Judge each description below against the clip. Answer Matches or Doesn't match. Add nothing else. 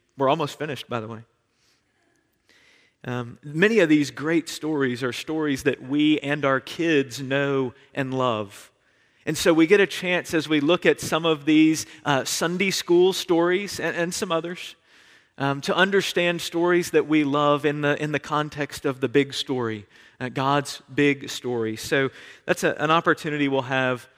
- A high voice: Doesn't match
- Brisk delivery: Doesn't match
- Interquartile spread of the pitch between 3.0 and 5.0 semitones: Matches